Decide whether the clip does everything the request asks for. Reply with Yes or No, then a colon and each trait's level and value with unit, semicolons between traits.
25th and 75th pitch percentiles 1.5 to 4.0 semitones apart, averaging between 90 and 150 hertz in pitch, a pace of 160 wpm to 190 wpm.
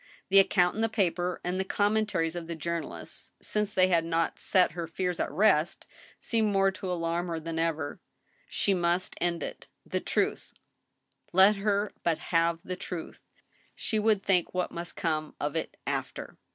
No: average, 2.9 semitones; medium, 180 Hz; average, 175 wpm